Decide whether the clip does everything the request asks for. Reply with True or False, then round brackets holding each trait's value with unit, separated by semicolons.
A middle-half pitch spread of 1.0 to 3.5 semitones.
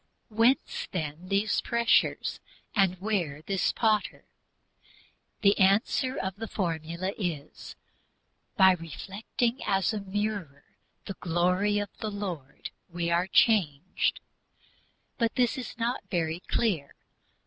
False (4.0 semitones)